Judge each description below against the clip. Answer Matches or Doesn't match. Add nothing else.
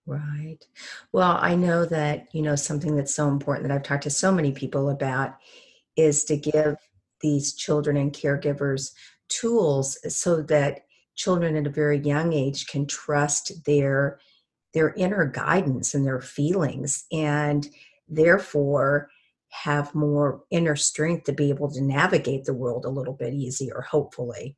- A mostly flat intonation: Matches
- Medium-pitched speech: Matches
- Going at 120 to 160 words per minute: Matches